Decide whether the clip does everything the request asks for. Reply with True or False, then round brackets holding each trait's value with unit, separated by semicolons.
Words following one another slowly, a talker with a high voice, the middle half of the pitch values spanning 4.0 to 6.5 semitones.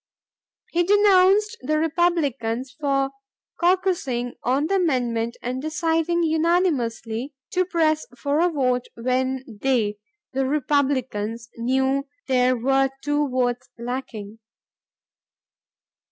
True (100 wpm; 270 Hz; 4.8 semitones)